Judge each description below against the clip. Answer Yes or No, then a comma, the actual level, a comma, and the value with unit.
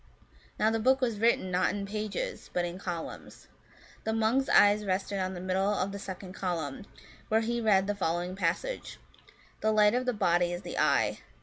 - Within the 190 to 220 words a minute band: Yes, average, 195 wpm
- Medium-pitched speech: No, high, 200 Hz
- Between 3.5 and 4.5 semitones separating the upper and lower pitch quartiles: No, average, 3.1 semitones